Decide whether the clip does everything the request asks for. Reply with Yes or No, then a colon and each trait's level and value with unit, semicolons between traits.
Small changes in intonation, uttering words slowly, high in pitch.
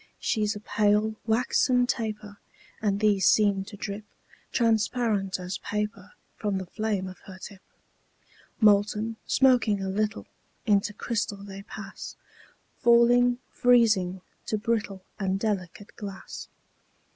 Yes: narrow, 2.1 semitones; slow, 120 wpm; high, 210 Hz